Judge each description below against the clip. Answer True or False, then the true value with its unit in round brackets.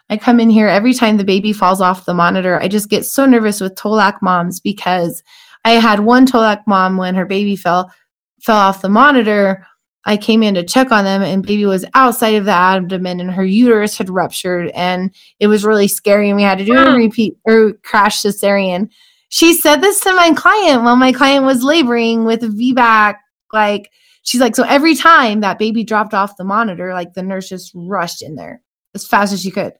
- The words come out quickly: True (210 wpm)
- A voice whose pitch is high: True (210 Hz)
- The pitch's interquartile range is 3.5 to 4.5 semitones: True (3.9 semitones)